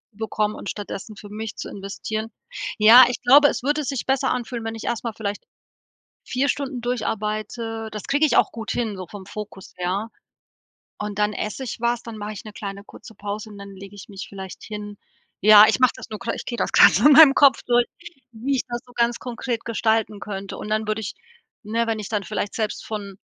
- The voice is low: No, high, 220 Hz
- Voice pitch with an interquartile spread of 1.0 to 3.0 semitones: Yes, narrow, 2.6 semitones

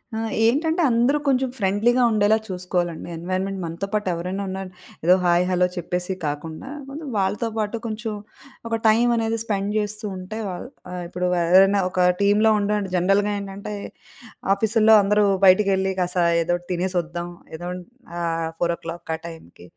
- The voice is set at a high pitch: Yes, high, 195 Hz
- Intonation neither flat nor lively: Yes, average, 3.3 semitones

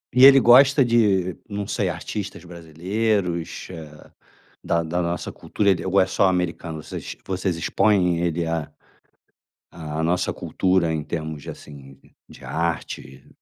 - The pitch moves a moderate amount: Yes, average, 3.3 semitones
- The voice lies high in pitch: No, very low, 90 Hz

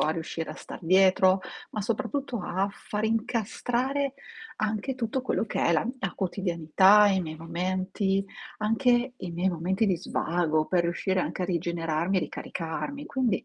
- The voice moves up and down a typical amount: Yes, average, 4.6 semitones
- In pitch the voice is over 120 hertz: Yes, high, 190 Hz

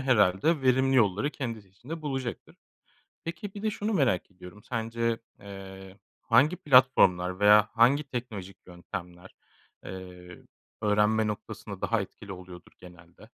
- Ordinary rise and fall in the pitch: No, wide, 5.8 semitones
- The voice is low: Yes, low, 105 Hz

